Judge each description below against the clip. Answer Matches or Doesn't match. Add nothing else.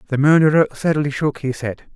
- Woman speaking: Doesn't match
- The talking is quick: Doesn't match